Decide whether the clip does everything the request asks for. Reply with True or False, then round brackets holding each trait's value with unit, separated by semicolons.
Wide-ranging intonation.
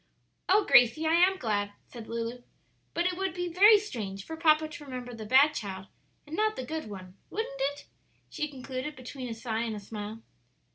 True (6.3 semitones)